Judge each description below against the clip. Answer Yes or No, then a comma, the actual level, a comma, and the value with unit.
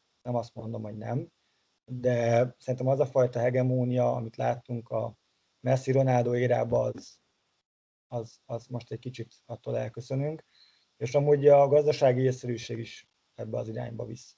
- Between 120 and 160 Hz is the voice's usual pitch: Yes, low, 125 Hz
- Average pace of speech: Yes, average, 145 wpm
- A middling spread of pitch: No, narrow, 2.1 semitones